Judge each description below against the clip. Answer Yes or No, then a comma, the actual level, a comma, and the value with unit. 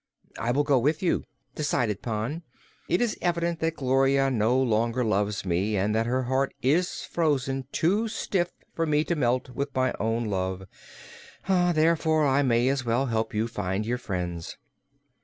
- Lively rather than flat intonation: Yes, wide, 5.7 semitones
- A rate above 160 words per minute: Yes, average, 175 wpm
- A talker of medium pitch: No, low, 130 Hz